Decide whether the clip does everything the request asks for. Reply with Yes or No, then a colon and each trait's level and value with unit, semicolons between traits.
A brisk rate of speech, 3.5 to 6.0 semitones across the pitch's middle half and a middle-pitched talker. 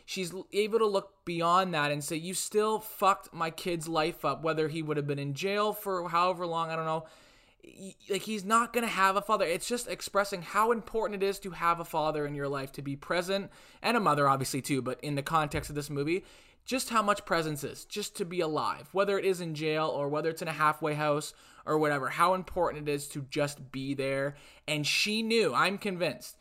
Yes: fast, 230 wpm; average, 4.8 semitones; medium, 165 Hz